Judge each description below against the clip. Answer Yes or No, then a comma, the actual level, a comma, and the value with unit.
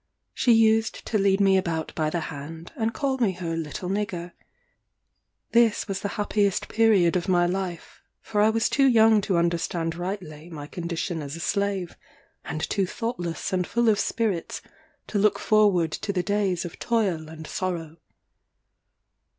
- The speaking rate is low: No, average, 165 wpm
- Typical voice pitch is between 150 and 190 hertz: Yes, medium, 185 Hz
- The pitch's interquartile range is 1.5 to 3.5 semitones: No, average, 4.0 semitones